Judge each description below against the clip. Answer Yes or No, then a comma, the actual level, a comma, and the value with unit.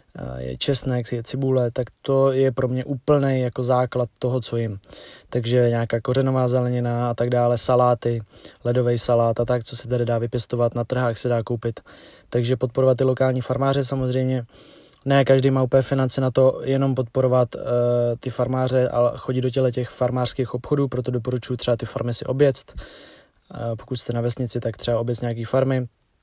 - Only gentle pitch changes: Yes, narrow, 1.5 semitones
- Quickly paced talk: Yes, fast, 180 wpm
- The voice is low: Yes, low, 125 Hz